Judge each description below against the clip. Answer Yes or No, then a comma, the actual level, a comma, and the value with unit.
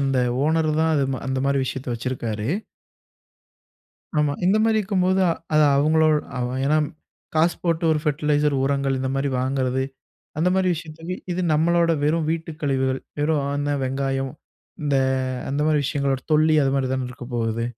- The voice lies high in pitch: No, medium, 145 Hz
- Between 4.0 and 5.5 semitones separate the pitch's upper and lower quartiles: No, average, 3.2 semitones